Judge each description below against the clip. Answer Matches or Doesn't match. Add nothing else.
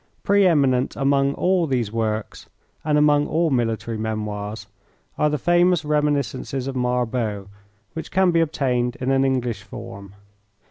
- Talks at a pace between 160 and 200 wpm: Doesn't match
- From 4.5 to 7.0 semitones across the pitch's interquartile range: Matches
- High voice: Doesn't match